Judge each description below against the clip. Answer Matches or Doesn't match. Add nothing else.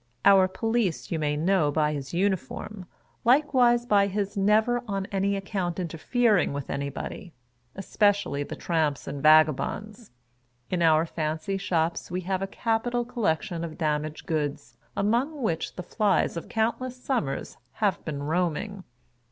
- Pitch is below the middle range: Doesn't match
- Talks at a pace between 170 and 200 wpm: Doesn't match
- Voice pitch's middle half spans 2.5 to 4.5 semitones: Doesn't match